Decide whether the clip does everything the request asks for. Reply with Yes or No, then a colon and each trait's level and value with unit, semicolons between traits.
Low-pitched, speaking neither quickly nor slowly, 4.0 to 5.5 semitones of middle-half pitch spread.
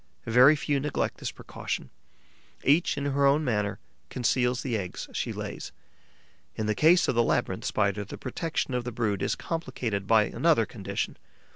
Yes: low, 125 Hz; average, 165 wpm; average, 4.7 semitones